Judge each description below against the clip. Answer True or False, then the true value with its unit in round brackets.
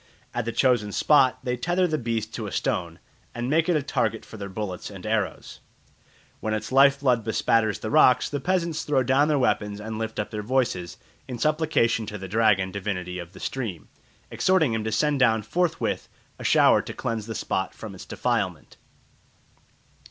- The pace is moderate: True (190 wpm)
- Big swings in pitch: False (4.8 semitones)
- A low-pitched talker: True (115 Hz)